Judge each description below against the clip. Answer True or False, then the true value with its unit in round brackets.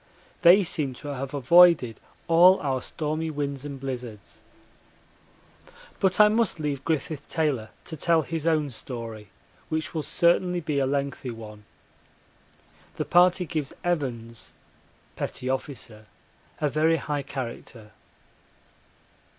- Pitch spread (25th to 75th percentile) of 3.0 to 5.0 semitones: True (4.2 semitones)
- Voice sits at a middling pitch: True (145 Hz)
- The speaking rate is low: True (120 wpm)